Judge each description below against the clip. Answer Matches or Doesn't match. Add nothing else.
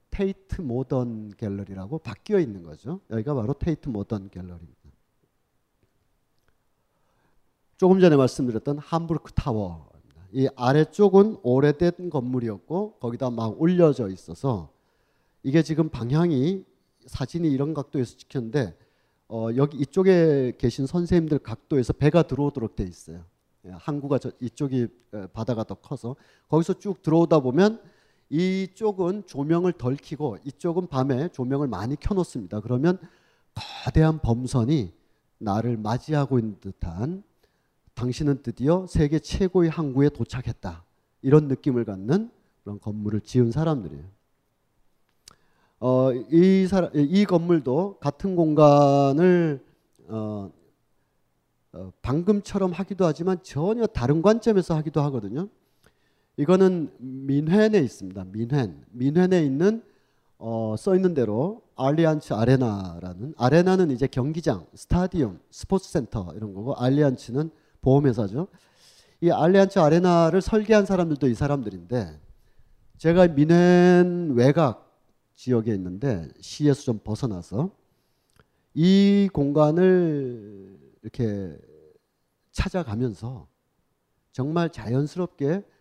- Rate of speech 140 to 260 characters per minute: Doesn't match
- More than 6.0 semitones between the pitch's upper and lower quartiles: Matches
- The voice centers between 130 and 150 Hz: Matches